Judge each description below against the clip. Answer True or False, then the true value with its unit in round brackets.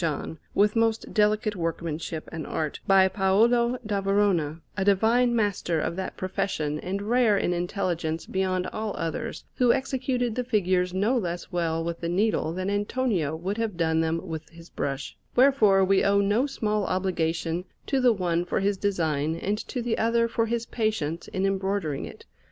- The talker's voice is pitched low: False (195 Hz)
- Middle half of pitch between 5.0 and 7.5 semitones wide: False (4.6 semitones)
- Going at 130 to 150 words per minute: False (175 wpm)